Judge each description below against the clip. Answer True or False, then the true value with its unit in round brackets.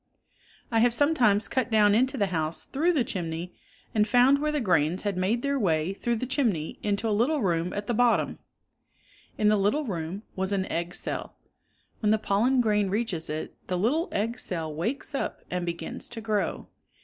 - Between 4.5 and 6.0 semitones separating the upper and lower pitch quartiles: True (5.2 semitones)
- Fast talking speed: False (195 wpm)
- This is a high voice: True (210 Hz)